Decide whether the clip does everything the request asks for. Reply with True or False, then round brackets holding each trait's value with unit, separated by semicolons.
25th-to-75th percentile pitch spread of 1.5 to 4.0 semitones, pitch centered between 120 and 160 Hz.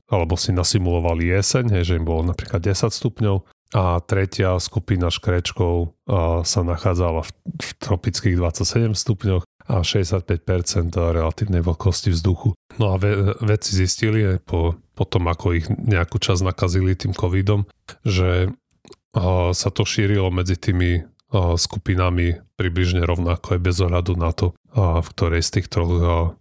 False (2.9 semitones; 95 Hz)